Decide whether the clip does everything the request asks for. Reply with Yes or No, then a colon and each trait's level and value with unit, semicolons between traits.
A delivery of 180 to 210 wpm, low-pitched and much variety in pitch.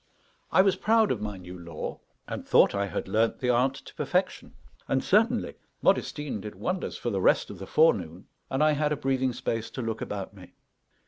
Yes: average, 200 wpm; low, 125 Hz; wide, 7.1 semitones